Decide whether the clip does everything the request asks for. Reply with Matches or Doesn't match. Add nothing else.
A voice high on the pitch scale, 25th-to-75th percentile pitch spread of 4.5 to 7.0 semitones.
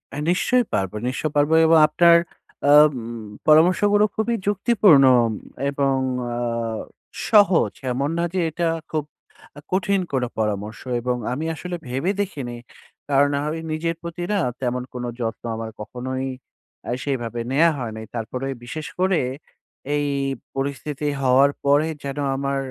Doesn't match